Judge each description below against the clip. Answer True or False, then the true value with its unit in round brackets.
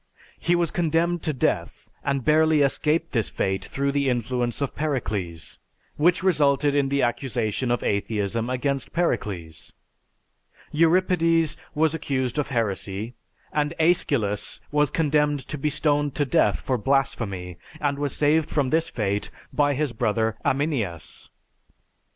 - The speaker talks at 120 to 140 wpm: True (135 wpm)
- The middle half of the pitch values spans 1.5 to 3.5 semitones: False (4.8 semitones)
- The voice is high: False (140 Hz)